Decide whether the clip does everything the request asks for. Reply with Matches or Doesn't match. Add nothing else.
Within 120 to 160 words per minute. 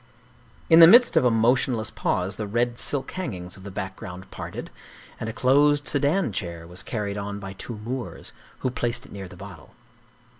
Doesn't match